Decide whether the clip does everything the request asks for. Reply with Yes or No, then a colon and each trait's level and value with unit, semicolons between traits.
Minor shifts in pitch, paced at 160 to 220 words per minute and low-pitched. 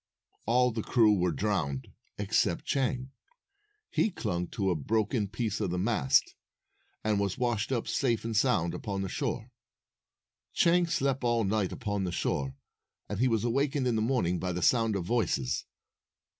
No: average, 4.6 semitones; average, 165 wpm; low, 110 Hz